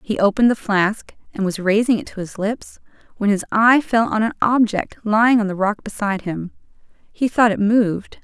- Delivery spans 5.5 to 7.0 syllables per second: No, 5.3 syllables/s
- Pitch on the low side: No, high, 210 Hz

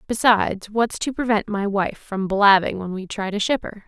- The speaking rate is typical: No, fast, 215 wpm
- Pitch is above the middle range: Yes, high, 205 Hz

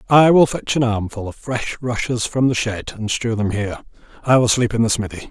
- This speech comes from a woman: No, male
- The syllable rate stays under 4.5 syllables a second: No, 5.4 syllables/s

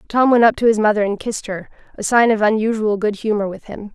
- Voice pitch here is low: No, high, 215 Hz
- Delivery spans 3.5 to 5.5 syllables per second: No, 6.2 syllables/s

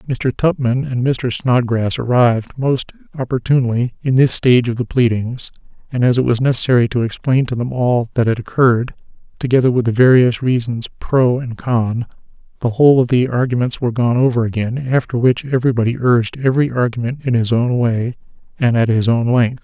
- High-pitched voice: No, low, 120 Hz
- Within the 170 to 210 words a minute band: Yes, average, 180 wpm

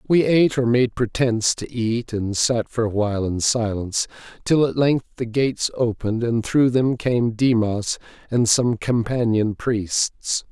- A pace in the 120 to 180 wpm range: Yes, average, 165 wpm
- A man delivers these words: Yes, male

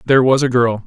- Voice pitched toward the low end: Yes, low, 125 Hz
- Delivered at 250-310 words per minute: Yes, fast, 280 wpm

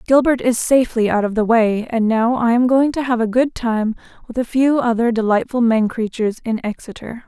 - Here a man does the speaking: No, female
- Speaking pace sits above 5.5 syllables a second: No, 5.4 syllables/s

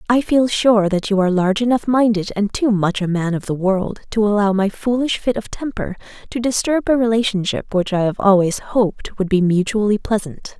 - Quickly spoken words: Yes, fast, 210 wpm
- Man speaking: No, female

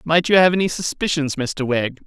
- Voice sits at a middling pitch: Yes, medium, 155 Hz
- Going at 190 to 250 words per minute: Yes, fast, 205 wpm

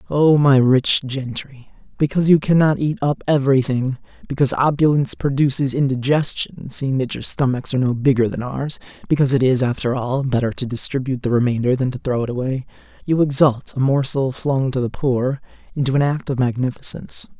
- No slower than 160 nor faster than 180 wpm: Yes, average, 175 wpm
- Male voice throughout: Yes, male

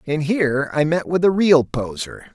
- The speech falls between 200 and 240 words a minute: Yes, fast, 205 wpm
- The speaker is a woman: No, male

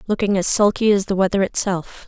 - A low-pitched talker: No, high, 195 Hz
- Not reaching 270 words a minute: Yes, average, 200 wpm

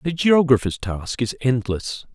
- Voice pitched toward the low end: Yes, low, 125 Hz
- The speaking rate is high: No, average, 140 wpm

